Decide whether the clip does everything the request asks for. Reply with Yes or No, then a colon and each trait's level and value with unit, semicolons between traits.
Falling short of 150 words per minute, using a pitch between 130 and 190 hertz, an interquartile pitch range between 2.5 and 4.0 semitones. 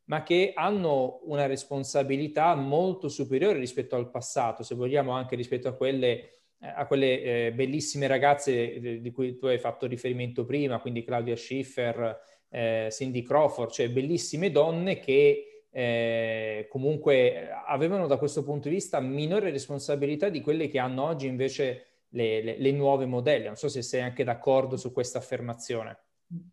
No: average, 155 wpm; low, 135 Hz; average, 3.1 semitones